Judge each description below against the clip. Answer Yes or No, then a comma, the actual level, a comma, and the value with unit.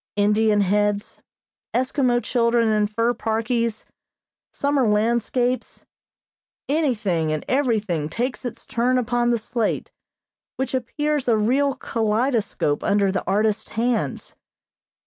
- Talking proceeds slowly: Yes, slow, 110 wpm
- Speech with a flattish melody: No, average, 3.0 semitones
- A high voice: Yes, high, 230 Hz